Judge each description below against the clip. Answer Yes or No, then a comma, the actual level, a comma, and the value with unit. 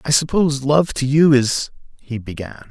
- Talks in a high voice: No, low, 135 Hz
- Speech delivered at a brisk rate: No, average, 175 wpm